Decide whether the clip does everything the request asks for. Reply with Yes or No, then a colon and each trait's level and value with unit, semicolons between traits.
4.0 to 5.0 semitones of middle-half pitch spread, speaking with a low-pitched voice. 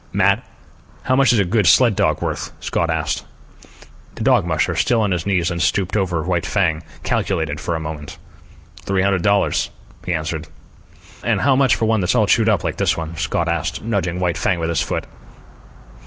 Yes: average, 4.3 semitones; very low, 90 Hz